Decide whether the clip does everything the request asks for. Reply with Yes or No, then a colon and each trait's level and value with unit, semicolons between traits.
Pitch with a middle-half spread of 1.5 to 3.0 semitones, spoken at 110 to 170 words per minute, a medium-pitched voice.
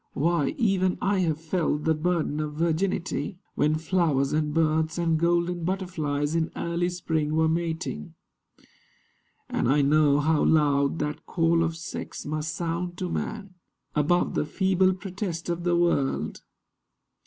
Yes: narrow, 2.5 semitones; average, 140 wpm; medium, 165 Hz